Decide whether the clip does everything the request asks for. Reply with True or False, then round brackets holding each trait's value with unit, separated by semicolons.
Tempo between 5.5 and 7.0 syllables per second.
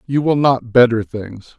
False (4.2 syllables/s)